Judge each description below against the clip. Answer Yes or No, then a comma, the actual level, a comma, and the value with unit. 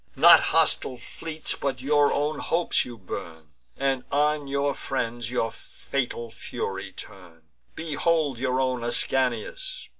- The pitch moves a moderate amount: Yes, average, 3.8 semitones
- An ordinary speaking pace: No, slow, 125 wpm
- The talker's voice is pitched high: No, low, 135 Hz